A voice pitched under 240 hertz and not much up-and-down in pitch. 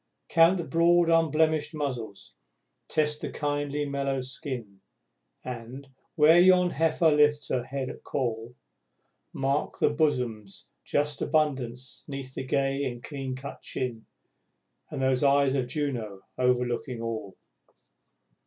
No: medium, 140 Hz; average, 3.2 semitones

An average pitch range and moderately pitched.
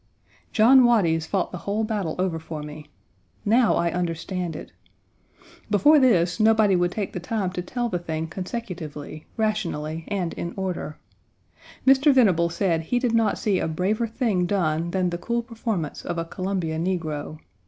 Yes: average, 4.7 semitones; medium, 180 Hz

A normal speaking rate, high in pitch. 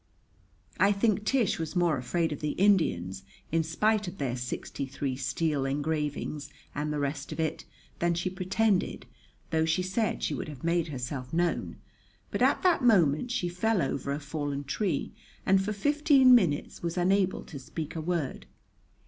No: average, 170 wpm; medium, 165 Hz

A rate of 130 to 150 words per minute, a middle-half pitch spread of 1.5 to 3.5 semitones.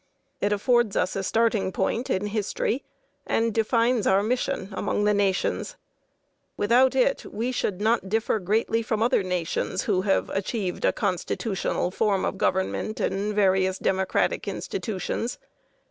Yes: average, 140 wpm; average, 3.1 semitones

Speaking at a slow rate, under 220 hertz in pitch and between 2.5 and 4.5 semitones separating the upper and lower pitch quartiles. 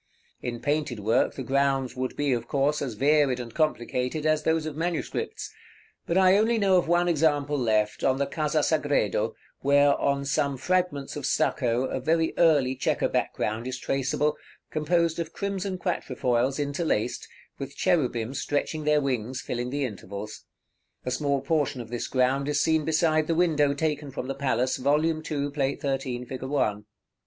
No: average, 170 wpm; medium, 140 Hz; average, 3.4 semitones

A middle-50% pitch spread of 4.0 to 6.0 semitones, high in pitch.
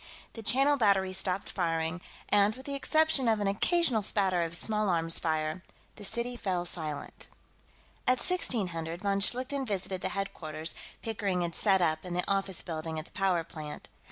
Yes: average, 4.7 semitones; high, 195 Hz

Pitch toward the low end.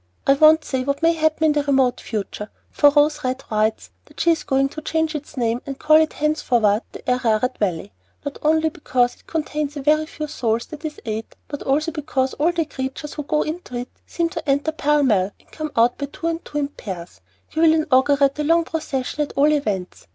No: very high, 290 Hz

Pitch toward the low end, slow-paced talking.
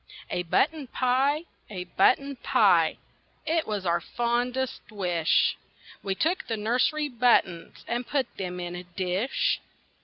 No: high, 235 Hz; slow, 130 wpm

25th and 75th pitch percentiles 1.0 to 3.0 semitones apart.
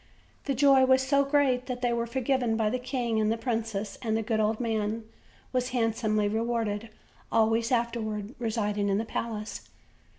Yes: narrow, 2.4 semitones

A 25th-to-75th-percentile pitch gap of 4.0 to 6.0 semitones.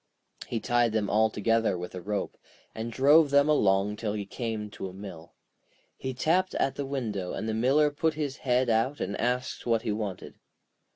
Yes: average, 4.5 semitones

